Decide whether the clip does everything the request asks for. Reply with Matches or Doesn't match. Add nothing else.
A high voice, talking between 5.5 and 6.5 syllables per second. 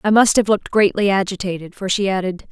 Matches